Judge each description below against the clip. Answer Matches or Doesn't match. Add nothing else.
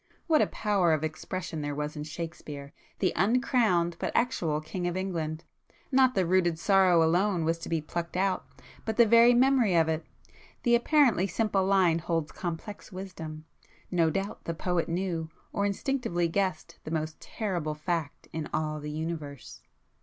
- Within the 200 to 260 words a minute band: Doesn't match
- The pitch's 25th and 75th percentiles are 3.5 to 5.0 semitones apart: Matches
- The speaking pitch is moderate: Matches